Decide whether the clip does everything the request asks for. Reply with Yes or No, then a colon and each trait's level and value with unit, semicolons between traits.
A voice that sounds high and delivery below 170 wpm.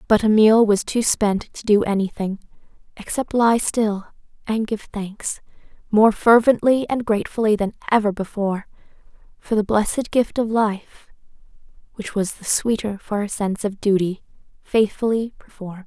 Yes: high, 210 Hz; average, 145 wpm